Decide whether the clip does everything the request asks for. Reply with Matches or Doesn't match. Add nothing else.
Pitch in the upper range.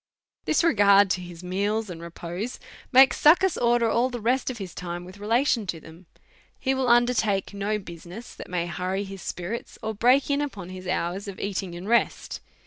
Matches